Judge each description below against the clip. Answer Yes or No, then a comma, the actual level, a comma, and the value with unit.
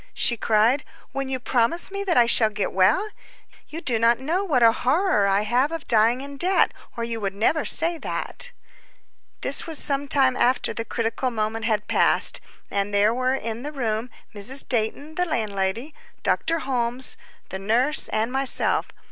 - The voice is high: Yes, high, 245 Hz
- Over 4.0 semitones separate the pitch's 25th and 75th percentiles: Yes, average, 4.4 semitones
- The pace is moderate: Yes, average, 175 wpm